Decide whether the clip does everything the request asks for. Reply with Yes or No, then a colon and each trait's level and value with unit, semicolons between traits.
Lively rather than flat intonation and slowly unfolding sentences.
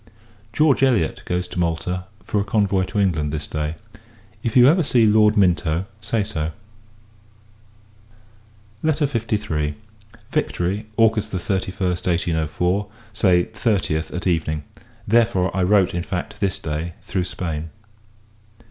No: average, 4.1 semitones; slow, 125 wpm